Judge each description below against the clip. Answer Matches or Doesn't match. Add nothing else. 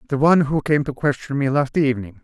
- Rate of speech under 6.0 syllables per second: Doesn't match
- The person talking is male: Matches